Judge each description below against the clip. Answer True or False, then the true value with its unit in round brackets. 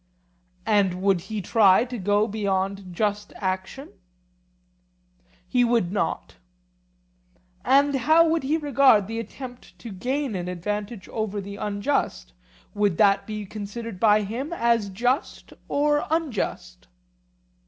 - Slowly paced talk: True (120 wpm)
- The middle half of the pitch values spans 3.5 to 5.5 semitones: True (4.1 semitones)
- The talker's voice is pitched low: False (215 Hz)